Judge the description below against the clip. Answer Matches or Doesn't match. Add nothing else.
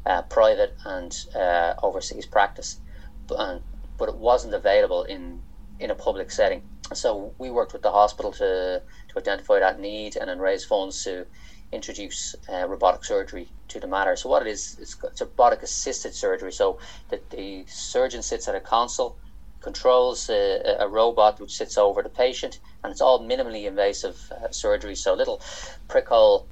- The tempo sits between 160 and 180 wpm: Matches